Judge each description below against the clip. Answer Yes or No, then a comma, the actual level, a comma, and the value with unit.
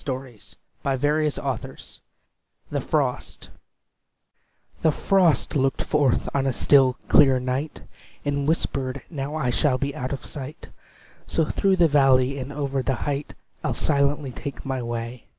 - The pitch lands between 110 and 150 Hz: Yes, medium, 140 Hz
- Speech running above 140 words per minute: No, slow, 135 wpm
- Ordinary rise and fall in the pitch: No, narrow, 2.3 semitones